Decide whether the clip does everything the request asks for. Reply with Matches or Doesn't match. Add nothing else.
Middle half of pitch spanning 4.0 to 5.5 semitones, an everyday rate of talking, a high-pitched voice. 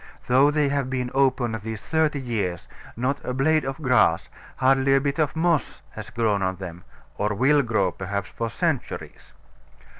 Doesn't match